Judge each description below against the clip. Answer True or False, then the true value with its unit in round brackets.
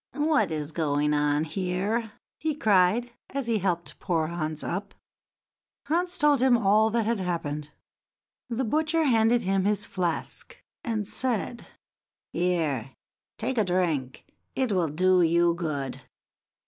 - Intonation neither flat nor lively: False (6.2 semitones)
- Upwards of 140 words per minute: False (135 wpm)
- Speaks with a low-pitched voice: False (190 Hz)